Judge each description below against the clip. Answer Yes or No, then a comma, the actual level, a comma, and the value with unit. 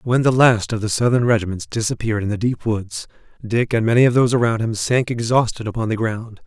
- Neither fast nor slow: No, fast, 225 wpm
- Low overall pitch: Yes, low, 115 Hz